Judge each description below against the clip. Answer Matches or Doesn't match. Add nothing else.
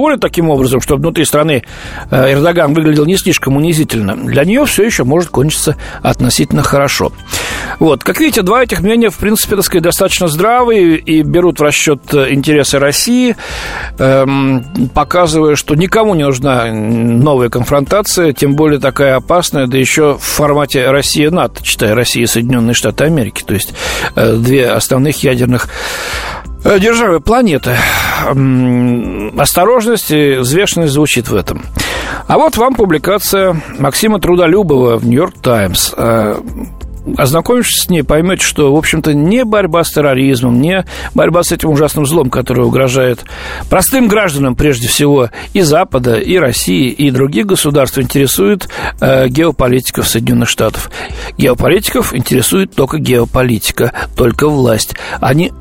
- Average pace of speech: Matches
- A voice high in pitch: Doesn't match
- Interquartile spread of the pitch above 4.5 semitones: Matches